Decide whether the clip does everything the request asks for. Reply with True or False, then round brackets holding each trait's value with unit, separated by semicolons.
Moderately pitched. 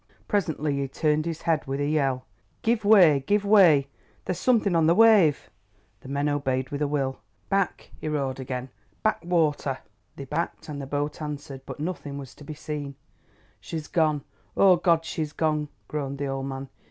True (150 Hz)